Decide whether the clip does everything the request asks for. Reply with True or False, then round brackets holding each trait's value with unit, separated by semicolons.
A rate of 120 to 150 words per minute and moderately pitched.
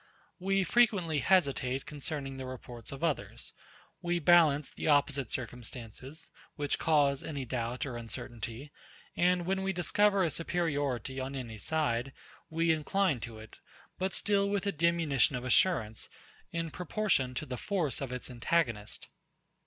True (145 wpm; 145 Hz)